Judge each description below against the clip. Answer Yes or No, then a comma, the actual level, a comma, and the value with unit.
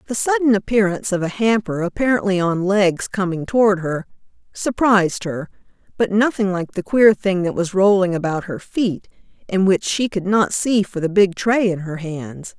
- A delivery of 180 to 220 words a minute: Yes, average, 185 wpm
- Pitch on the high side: Yes, high, 195 Hz